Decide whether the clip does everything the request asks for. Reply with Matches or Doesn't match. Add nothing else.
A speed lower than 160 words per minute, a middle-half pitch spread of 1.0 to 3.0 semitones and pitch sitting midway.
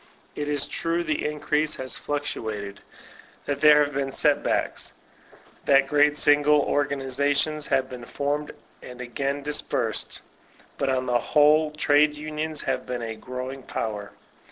Matches